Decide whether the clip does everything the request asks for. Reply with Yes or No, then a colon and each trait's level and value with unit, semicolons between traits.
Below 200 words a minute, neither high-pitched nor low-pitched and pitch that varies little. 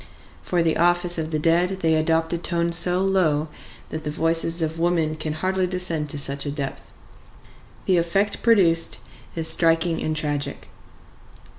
Yes: average, 160 wpm; medium, 165 Hz; narrow, 2.0 semitones